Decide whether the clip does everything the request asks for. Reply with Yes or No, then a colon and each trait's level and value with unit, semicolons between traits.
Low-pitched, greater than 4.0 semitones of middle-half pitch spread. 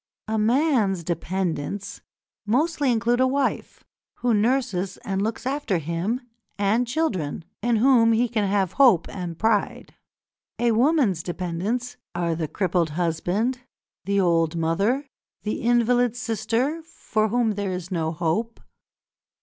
No: high, 215 Hz; wide, 5.4 semitones